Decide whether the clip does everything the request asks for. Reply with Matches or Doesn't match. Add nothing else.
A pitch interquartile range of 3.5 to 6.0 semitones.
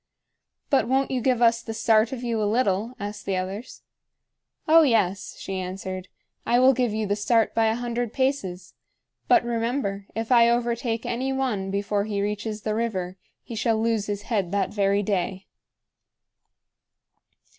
Doesn't match